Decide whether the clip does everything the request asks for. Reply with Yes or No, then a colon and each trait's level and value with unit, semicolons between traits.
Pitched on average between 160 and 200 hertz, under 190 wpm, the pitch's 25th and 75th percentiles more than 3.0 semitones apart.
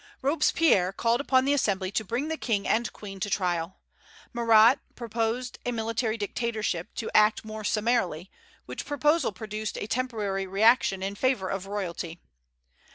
No: high, 220 Hz; average, 150 wpm; average, 3.7 semitones